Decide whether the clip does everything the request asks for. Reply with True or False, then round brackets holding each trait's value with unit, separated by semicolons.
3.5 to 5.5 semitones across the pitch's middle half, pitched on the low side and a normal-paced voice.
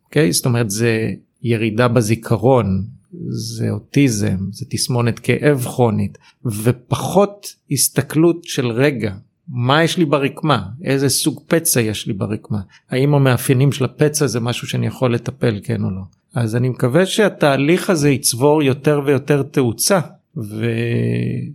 True (4.1 semitones; 130 Hz; 135 wpm)